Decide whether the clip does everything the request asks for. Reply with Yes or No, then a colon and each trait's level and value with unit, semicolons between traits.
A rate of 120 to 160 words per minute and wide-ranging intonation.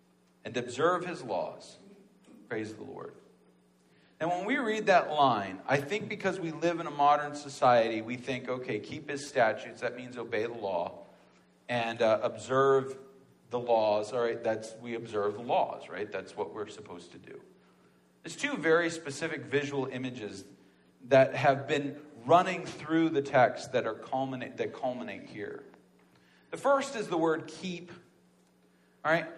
Yes: average, 155 wpm; wide, 7.3 semitones